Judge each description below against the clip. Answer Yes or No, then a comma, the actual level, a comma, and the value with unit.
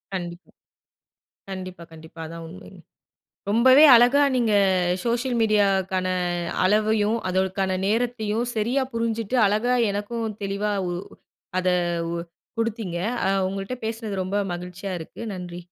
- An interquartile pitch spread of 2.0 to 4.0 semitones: Yes, average, 3.6 semitones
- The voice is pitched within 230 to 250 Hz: No, high, 205 Hz